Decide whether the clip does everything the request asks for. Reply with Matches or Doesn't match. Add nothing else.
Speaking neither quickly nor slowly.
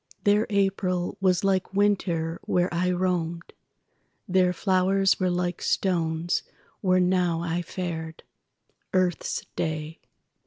Doesn't match